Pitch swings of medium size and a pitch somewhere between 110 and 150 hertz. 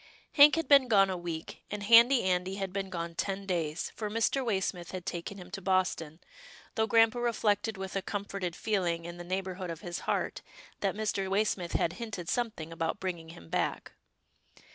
No: average, 3.5 semitones; high, 190 Hz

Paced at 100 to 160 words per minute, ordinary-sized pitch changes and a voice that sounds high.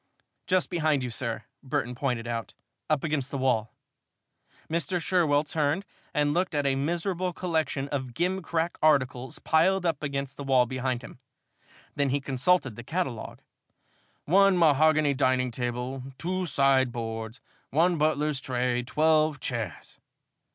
No: slow, 135 wpm; average, 4.1 semitones; medium, 140 Hz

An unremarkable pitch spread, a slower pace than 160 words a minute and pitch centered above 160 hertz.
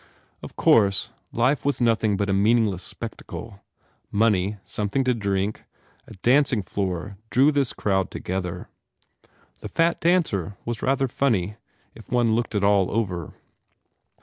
No: average, 3.8 semitones; slow, 135 wpm; low, 105 Hz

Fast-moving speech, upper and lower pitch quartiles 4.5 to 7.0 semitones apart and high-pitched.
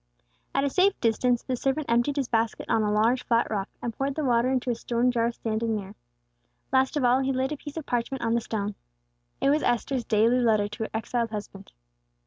No: fast, 220 wpm; average, 3.0 semitones; high, 240 Hz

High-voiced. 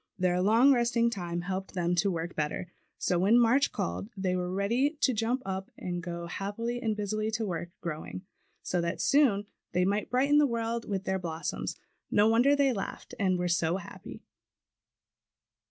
Yes: high, 195 Hz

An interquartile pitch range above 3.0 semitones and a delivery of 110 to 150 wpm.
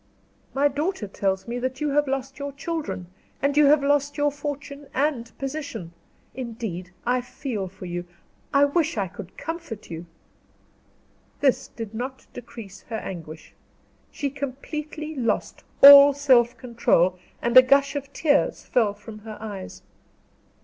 Yes: average, 5.0 semitones; average, 145 wpm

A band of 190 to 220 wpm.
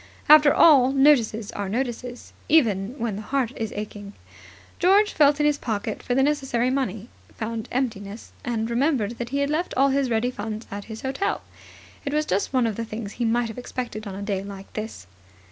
Yes: average, 195 wpm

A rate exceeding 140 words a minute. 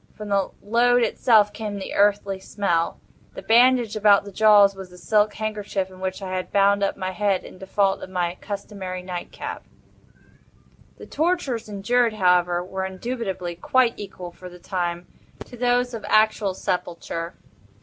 Yes: average, 160 wpm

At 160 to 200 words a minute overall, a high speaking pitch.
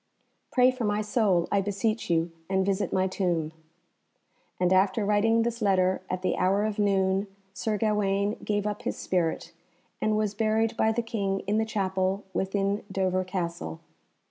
Yes: average, 165 wpm; high, 200 Hz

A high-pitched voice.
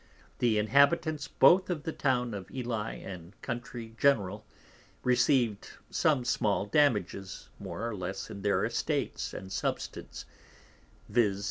No: low, 115 Hz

